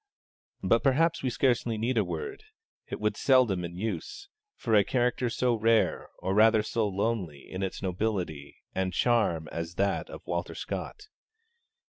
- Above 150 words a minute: Yes, average, 160 wpm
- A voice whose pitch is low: Yes, low, 110 Hz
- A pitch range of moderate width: Yes, average, 4.7 semitones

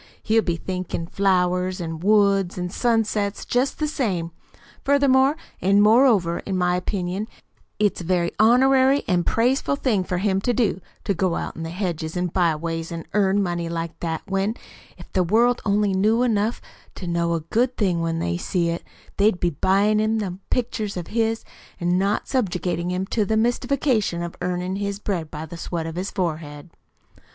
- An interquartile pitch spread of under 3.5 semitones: No, average, 4.0 semitones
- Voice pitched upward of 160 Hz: Yes, high, 190 Hz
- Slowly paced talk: No, average, 180 wpm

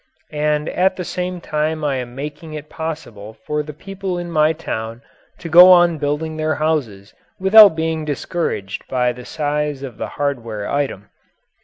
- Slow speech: No, average, 165 wpm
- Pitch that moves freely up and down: No, average, 3.4 semitones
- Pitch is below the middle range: No, medium, 150 Hz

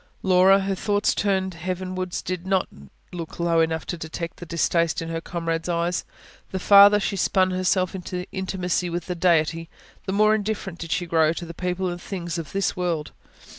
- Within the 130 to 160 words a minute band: No, average, 190 wpm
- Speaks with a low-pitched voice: No, medium, 180 Hz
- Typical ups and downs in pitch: No, narrow, 2.1 semitones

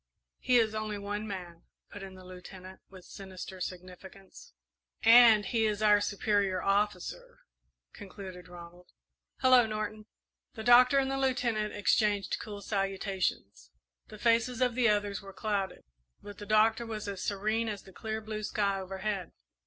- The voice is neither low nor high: No, high, 205 Hz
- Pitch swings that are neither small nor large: No, narrow, 2.3 semitones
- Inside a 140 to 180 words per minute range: Yes, average, 150 wpm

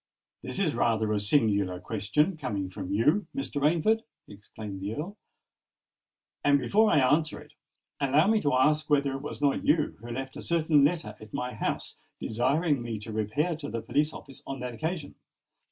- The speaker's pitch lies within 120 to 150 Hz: Yes, medium, 140 Hz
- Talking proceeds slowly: No, average, 175 wpm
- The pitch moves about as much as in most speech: No, wide, 5.8 semitones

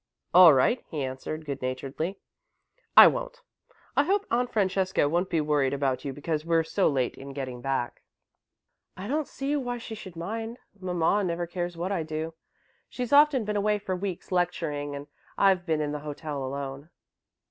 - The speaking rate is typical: Yes, average, 175 wpm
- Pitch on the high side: No, medium, 170 Hz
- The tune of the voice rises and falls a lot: Yes, wide, 6.1 semitones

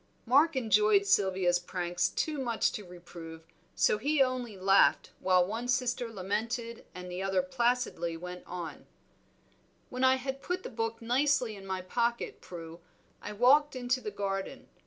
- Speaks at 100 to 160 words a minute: Yes, average, 155 wpm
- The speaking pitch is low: No, high, 220 Hz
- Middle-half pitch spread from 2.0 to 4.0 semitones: No, average, 5.3 semitones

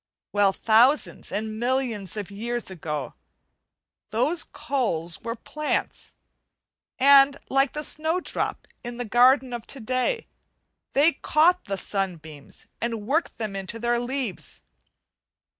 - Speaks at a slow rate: Yes, slow, 120 wpm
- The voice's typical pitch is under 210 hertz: No, high, 240 Hz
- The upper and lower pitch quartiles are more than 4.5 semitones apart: Yes, average, 5.0 semitones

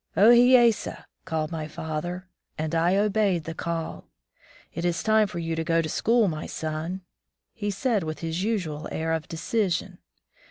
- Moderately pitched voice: Yes, medium, 170 Hz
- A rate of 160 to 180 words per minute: Yes, average, 175 wpm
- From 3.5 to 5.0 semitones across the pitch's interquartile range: Yes, average, 4.3 semitones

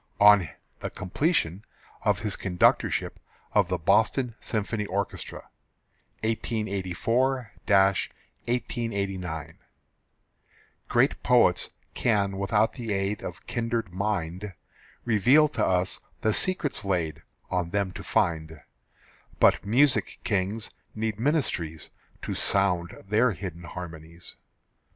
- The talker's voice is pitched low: Yes, low, 100 Hz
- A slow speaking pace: Yes, slow, 100 wpm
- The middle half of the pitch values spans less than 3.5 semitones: No, average, 3.9 semitones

